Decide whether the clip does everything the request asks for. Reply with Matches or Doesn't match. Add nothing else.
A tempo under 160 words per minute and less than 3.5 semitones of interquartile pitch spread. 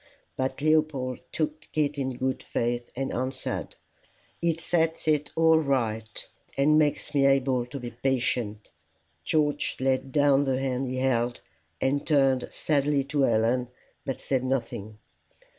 Matches